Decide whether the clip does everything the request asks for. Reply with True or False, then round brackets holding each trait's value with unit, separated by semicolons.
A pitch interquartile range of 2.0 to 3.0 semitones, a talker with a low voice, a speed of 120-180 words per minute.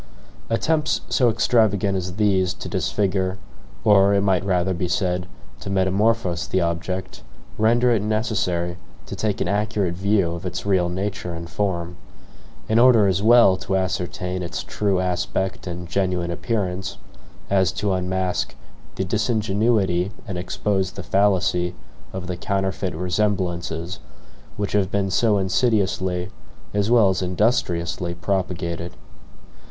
True (2.5 semitones; 95 Hz; 135 wpm)